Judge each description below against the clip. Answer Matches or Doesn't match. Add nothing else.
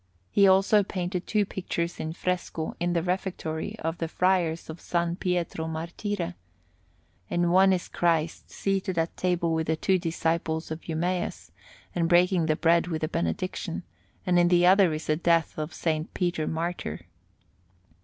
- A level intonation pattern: Matches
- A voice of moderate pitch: Matches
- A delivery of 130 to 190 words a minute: Matches